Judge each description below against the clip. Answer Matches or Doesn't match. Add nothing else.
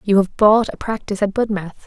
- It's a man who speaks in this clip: Doesn't match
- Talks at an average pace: Doesn't match